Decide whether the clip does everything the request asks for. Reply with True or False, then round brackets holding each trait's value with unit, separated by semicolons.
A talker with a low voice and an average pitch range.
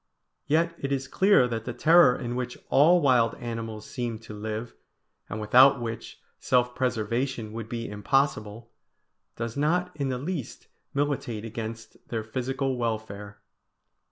True (120 Hz; 3.3 semitones)